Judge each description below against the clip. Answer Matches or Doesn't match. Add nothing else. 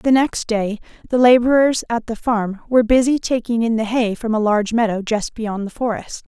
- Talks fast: Matches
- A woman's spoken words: Matches